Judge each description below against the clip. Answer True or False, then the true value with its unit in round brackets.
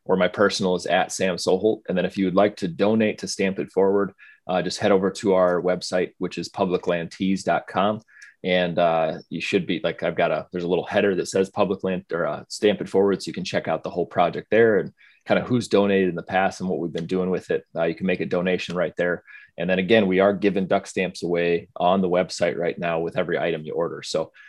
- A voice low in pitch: True (95 Hz)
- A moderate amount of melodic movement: False (1.8 semitones)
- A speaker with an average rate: False (250 wpm)